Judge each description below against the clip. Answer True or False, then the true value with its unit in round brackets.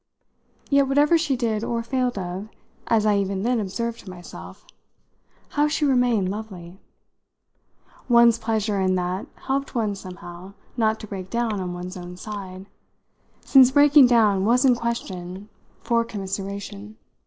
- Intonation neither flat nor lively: True (4.1 semitones)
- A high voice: True (215 Hz)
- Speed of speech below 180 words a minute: True (145 wpm)